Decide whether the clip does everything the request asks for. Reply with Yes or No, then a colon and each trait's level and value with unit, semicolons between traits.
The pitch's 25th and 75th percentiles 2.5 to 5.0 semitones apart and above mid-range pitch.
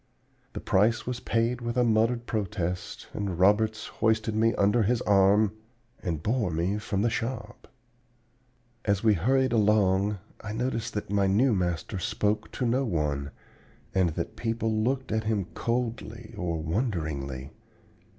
No: average, 3.3 semitones; low, 105 Hz